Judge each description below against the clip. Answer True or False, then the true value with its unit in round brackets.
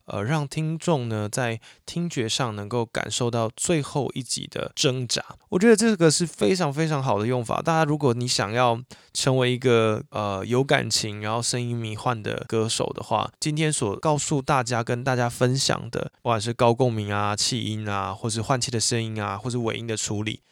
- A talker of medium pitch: False (125 Hz)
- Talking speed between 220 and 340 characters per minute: True (290 characters per minute)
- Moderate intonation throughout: True (4.5 semitones)